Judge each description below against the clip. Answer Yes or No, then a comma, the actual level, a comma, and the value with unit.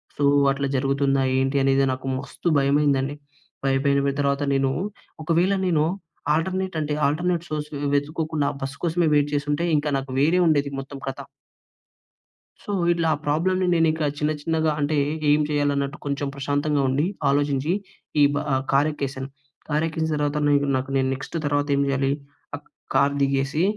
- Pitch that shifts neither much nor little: No, narrow, 2.1 semitones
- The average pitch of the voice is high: No, medium, 145 Hz